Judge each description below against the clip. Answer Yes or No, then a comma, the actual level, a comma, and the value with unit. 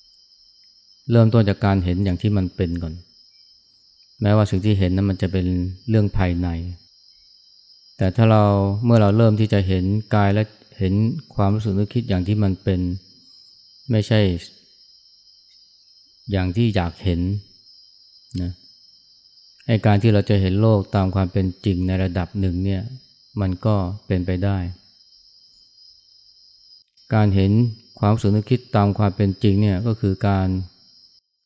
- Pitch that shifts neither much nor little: No, narrow, 2.2 semitones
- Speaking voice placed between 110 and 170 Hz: No, low, 100 Hz